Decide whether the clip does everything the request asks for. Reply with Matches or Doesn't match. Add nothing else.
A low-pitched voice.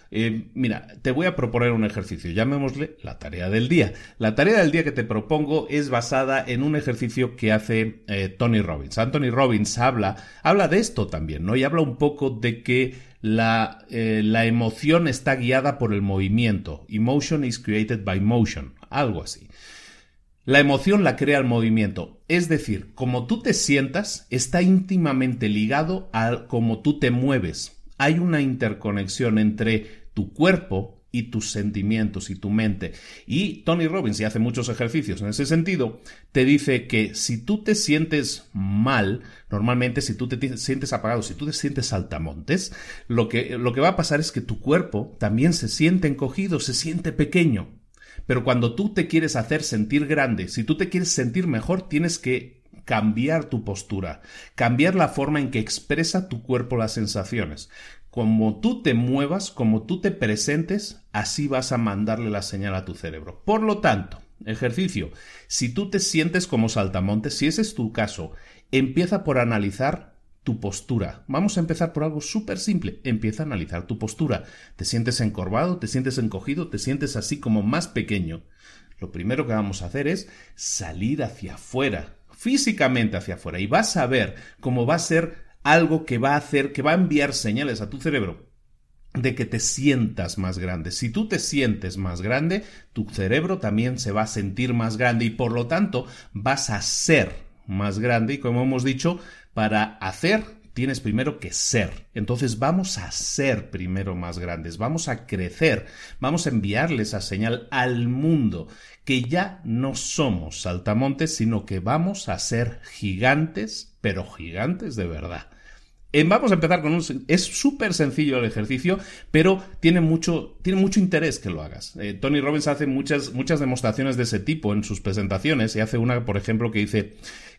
Matches